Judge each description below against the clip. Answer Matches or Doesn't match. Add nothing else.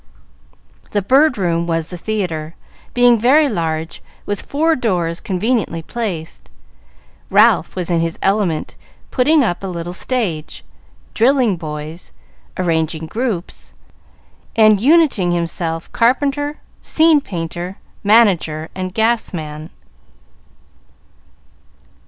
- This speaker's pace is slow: Matches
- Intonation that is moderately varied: Doesn't match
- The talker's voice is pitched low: Doesn't match